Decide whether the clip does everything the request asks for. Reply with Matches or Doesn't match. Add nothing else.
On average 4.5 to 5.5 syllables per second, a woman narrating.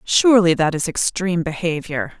Matches